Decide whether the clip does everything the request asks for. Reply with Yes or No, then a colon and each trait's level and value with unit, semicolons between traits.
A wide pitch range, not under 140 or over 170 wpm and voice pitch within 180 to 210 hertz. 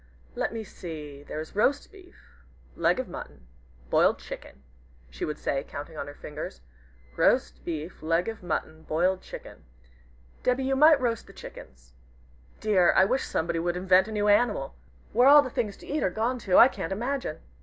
No: wide, 7.4 semitones; average, 180 wpm; medium, 185 Hz